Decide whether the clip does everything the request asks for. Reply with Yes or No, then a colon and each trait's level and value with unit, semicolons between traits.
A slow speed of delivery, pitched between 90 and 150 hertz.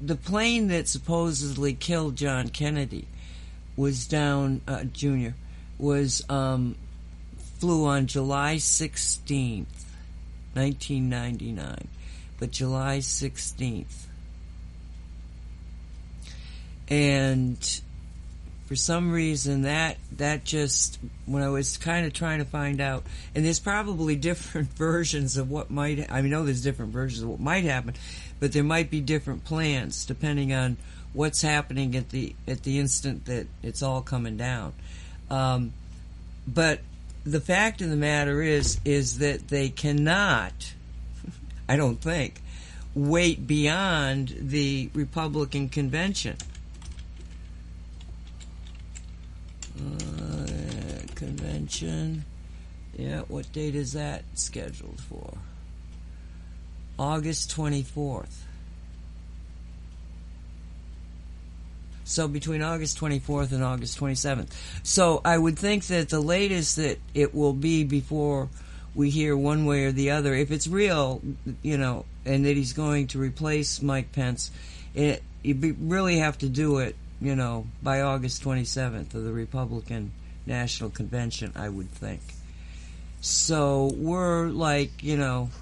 Yes: slow, 125 wpm; low, 135 Hz